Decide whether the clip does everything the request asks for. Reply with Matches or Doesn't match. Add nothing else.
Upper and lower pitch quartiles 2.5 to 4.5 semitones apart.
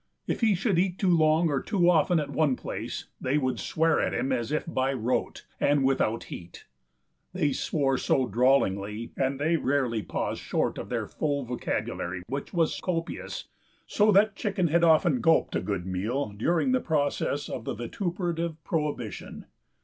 Doesn't match